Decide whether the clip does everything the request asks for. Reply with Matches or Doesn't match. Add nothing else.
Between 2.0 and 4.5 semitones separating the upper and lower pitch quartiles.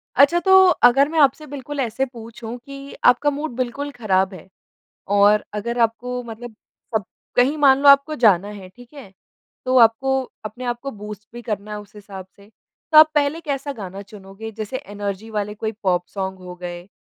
Doesn't match